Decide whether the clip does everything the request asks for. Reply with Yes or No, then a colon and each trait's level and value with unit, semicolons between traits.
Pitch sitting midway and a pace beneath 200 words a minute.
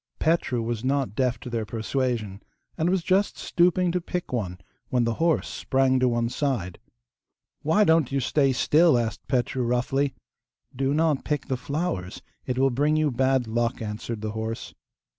No: low, 130 Hz; average, 170 wpm